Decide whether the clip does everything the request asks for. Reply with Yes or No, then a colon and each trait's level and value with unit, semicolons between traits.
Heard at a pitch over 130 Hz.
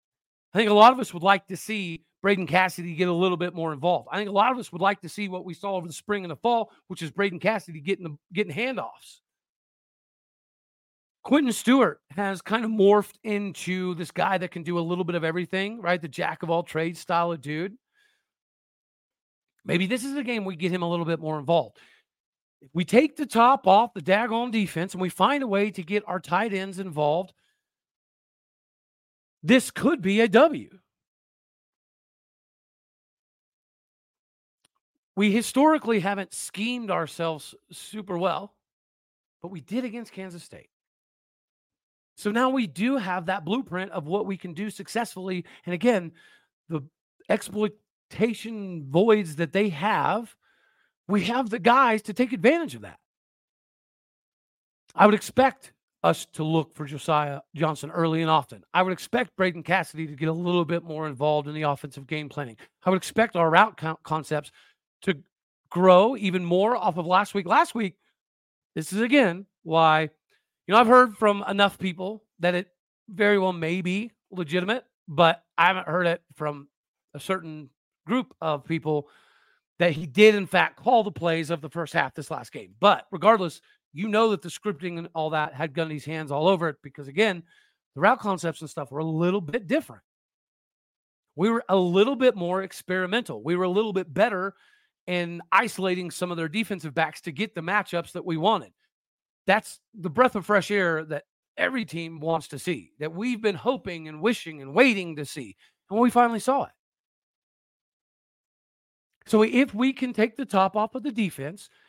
Yes: medium, 185 Hz